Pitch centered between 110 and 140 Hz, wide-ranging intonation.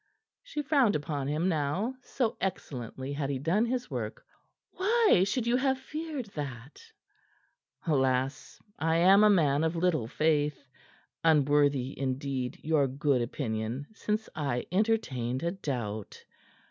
No: medium, 150 Hz; wide, 7.7 semitones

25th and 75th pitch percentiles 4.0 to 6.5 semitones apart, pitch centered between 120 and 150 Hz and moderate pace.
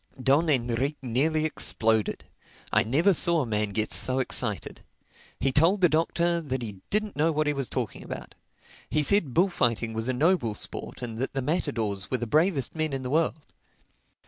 Yes: average, 5.3 semitones; low, 135 Hz; average, 180 wpm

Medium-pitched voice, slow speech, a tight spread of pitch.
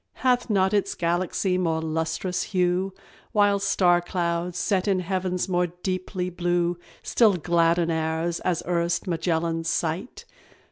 Yes: medium, 175 Hz; slow, 130 wpm; narrow, 1.8 semitones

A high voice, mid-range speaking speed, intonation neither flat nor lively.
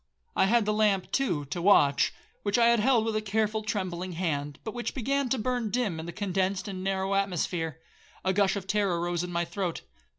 No: high, 195 Hz; fast, 210 wpm; average, 3.6 semitones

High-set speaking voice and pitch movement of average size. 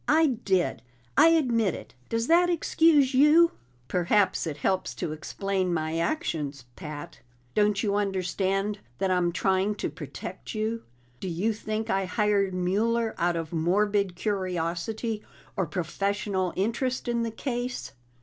Yes: high, 200 Hz; average, 4.3 semitones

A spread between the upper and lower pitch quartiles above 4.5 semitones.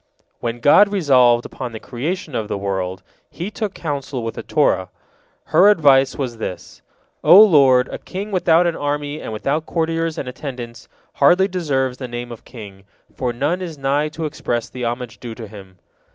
Yes: wide, 5.4 semitones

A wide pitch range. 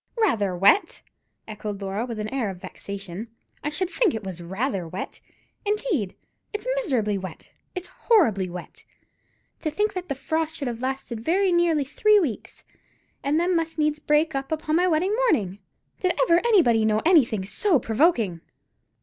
Yes: wide, 8.8 semitones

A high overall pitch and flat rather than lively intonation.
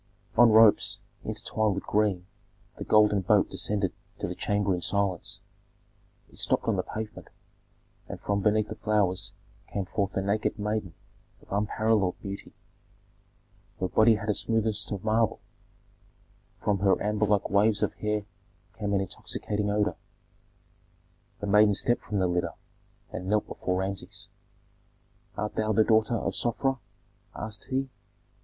No: low, 105 Hz; narrow, 1.6 semitones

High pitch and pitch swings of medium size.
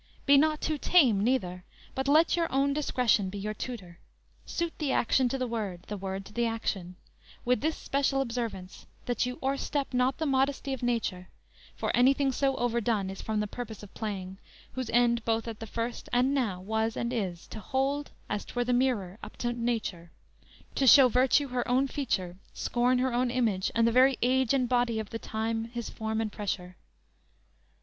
Yes: high, 240 Hz; average, 3.7 semitones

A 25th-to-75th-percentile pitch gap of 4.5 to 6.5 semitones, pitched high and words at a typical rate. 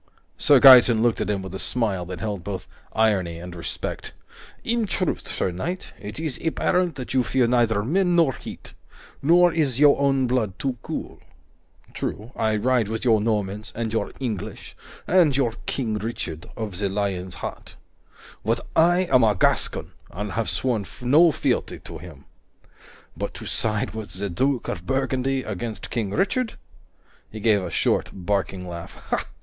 No: average, 5.0 semitones; low, 115 Hz; average, 165 wpm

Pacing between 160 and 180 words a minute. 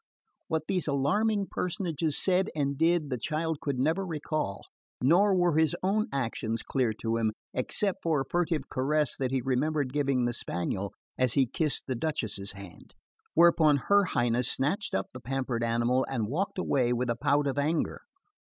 Yes: average, 170 wpm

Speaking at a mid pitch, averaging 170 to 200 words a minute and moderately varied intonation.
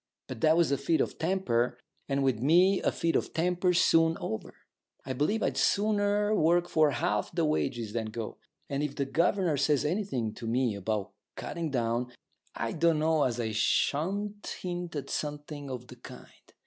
No: medium, 150 Hz; average, 180 wpm; wide, 5.8 semitones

